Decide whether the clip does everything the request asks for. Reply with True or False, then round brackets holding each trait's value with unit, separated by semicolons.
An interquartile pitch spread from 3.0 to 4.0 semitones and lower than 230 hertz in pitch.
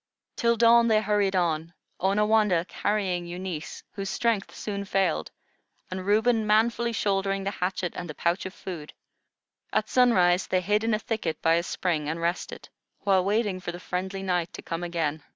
True (3.3 semitones; 190 Hz)